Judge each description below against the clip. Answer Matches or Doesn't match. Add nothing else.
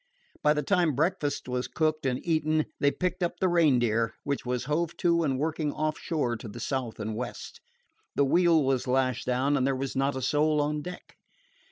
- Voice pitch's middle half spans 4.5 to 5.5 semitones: Doesn't match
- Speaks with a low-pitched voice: Doesn't match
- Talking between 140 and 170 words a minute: Doesn't match